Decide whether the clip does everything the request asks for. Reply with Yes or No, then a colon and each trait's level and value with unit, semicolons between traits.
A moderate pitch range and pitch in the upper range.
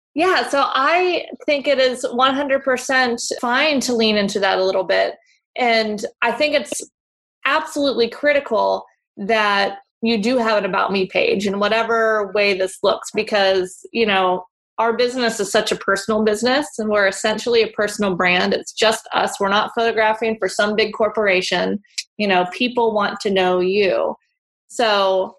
Yes: average, 3.7 semitones; high, 220 Hz